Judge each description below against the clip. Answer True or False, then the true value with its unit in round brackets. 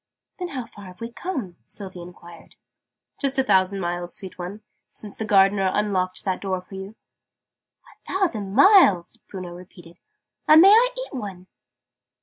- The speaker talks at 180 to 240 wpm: False (155 wpm)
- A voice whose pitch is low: False (195 Hz)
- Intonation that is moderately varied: True (4.7 semitones)